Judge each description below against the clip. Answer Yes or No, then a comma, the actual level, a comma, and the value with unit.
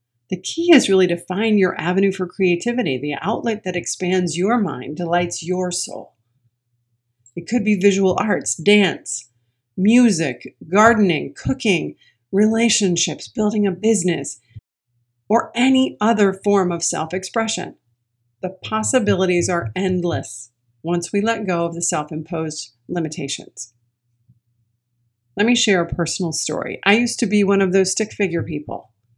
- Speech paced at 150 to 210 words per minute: No, average, 140 wpm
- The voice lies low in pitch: No, medium, 180 Hz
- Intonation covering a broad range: Yes, wide, 8.2 semitones